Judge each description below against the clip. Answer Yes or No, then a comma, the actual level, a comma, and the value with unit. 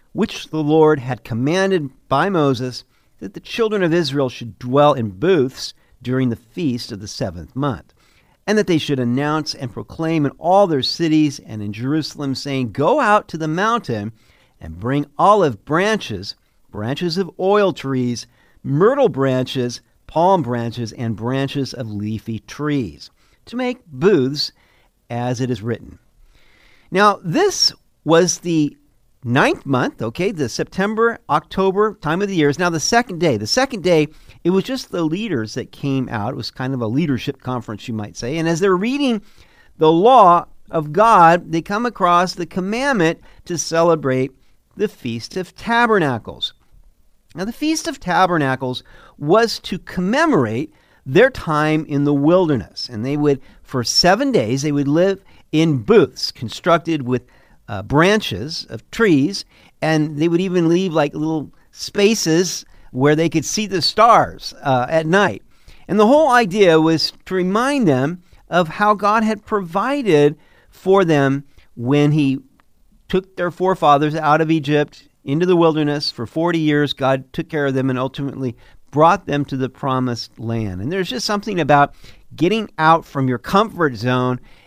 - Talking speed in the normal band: Yes, average, 160 wpm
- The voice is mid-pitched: Yes, medium, 150 Hz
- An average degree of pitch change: No, wide, 6.0 semitones